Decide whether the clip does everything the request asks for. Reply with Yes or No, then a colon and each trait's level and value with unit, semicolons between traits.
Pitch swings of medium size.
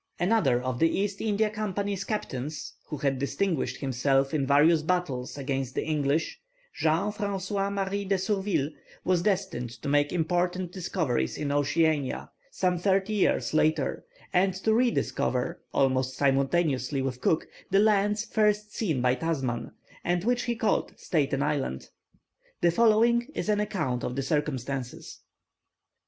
No: wide, 6.6 semitones